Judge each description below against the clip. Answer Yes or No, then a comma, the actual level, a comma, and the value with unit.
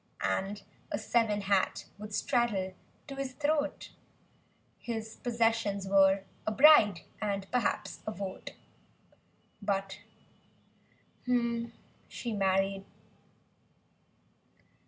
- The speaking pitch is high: Yes, high, 205 Hz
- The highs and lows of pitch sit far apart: No, average, 3.3 semitones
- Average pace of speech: No, slow, 80 wpm